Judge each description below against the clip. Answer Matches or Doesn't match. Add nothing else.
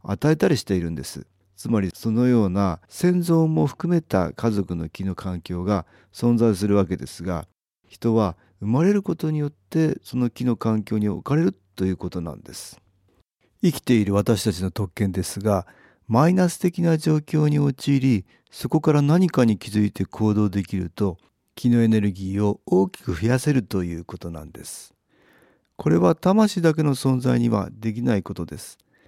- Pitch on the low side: Matches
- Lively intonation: Matches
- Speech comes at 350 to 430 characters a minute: Doesn't match